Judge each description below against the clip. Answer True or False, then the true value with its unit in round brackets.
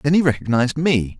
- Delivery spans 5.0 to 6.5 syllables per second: True (6.1 syllables/s)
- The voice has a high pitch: False (135 Hz)